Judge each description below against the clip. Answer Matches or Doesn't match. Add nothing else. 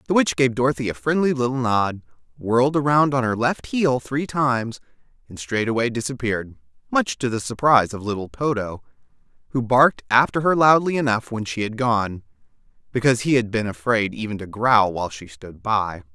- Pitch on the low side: Matches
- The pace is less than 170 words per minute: Doesn't match